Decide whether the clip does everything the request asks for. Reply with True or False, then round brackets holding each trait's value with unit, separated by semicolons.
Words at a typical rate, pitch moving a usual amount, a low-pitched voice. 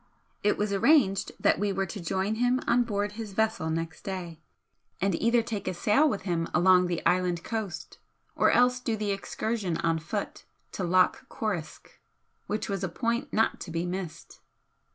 False (175 wpm; 3.9 semitones; 195 Hz)